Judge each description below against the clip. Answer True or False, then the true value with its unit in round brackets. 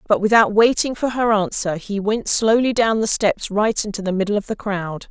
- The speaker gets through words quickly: True (225 wpm)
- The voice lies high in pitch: True (210 Hz)